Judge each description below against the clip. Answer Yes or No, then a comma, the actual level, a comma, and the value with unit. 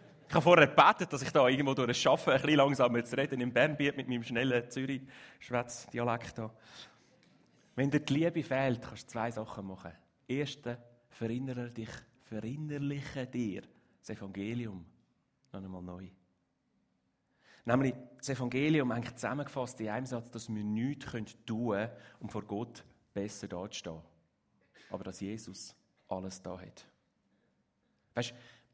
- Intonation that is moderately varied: Yes, average, 3.8 semitones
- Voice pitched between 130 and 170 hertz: No, low, 120 Hz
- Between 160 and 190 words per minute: No, average, 140 wpm